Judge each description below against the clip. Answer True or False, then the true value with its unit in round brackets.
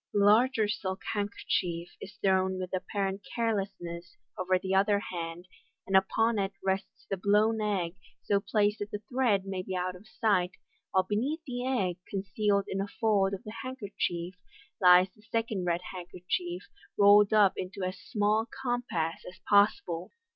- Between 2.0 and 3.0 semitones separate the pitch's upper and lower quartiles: True (2.4 semitones)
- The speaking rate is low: False (160 wpm)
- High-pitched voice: True (195 Hz)